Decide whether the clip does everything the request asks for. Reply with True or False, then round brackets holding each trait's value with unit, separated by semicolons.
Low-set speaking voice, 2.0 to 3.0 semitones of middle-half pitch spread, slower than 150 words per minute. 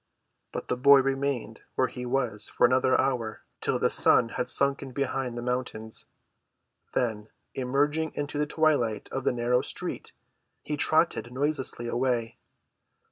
True (130 Hz; 2.7 semitones; 140 wpm)